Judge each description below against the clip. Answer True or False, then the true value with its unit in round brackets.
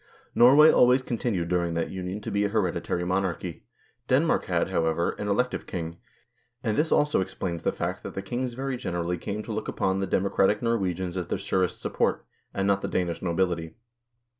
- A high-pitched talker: False (95 Hz)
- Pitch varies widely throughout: False (3.9 semitones)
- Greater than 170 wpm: True (190 wpm)